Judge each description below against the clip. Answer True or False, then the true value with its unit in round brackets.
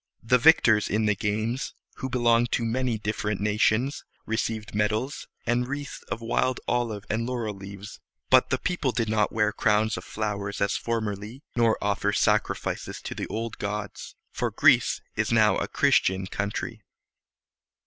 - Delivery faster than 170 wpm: False (155 wpm)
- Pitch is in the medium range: False (110 Hz)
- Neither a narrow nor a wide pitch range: False (2.3 semitones)